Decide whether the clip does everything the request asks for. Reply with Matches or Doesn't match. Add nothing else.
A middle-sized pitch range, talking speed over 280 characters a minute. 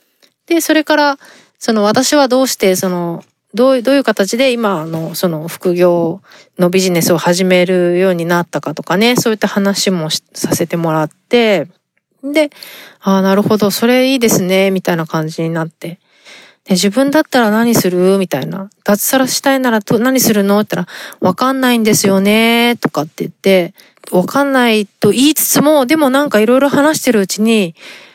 Doesn't match